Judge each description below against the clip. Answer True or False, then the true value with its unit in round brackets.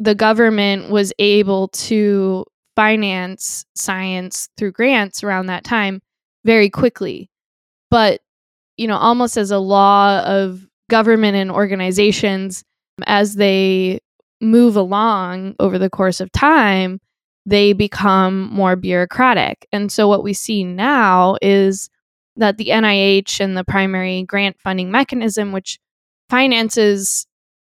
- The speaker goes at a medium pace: False (120 wpm)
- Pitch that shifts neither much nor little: False (2.0 semitones)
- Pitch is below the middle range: False (200 Hz)